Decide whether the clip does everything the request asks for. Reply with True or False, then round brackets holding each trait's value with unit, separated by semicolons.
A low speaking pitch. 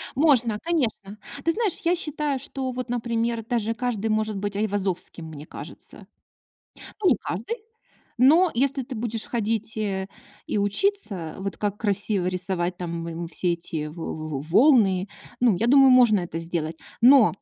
False (215 Hz)